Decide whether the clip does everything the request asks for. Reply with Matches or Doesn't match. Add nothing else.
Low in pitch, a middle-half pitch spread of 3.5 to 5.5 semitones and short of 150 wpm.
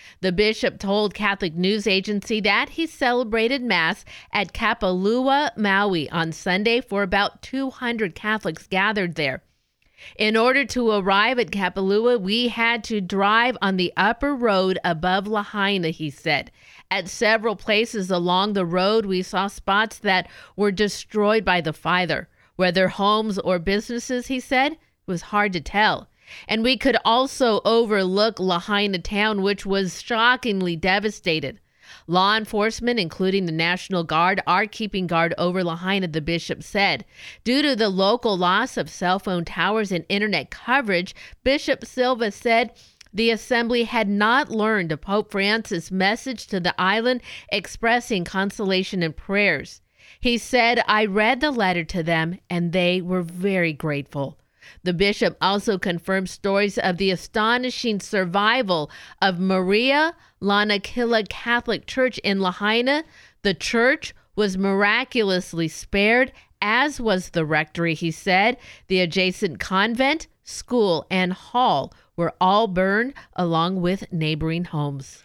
Doesn't match